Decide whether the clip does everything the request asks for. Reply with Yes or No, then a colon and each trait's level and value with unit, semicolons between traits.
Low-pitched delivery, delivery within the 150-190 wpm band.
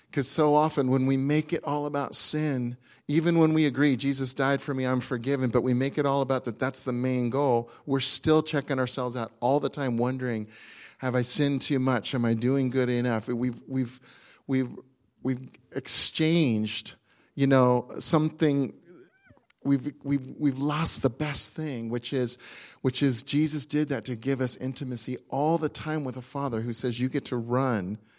Yes: low, 130 Hz; average, 185 wpm